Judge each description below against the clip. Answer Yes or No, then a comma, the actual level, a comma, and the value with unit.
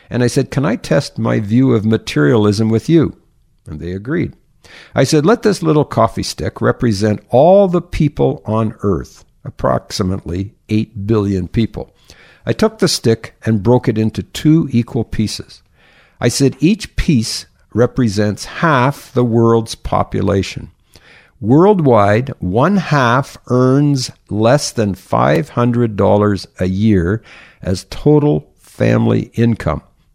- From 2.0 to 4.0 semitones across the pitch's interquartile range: No, average, 5.2 semitones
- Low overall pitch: Yes, low, 115 Hz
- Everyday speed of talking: No, slow, 130 wpm